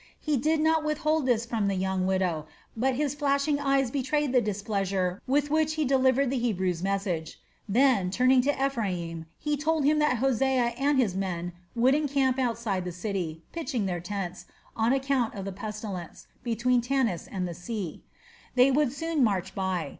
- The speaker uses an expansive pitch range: Yes, wide, 6.4 semitones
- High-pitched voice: Yes, high, 240 Hz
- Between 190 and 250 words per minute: No, average, 175 wpm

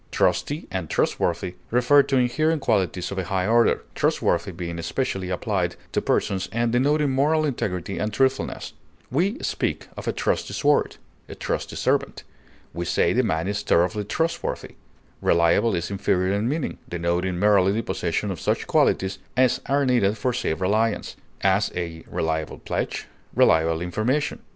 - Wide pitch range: Yes, wide, 6.3 semitones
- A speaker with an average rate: Yes, average, 155 wpm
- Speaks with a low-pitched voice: Yes, low, 100 Hz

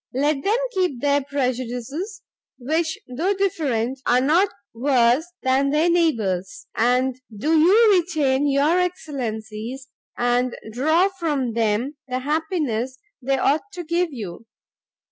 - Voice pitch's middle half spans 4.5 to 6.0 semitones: Yes, average, 4.9 semitones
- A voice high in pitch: Yes, very high, 275 Hz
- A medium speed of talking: No, slow, 125 wpm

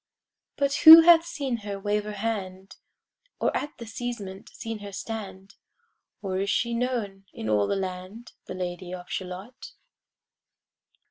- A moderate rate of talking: Yes, average, 145 wpm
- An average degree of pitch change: Yes, average, 3.9 semitones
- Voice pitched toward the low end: No, high, 205 Hz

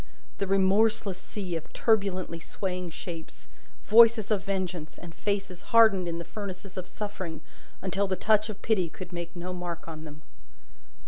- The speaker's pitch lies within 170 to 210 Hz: Yes, medium, 185 Hz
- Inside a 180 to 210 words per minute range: No, average, 155 wpm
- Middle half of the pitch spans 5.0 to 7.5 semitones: No, average, 2.8 semitones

